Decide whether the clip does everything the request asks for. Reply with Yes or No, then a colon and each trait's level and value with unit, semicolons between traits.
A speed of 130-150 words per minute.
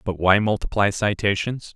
Yes: slow, 135 wpm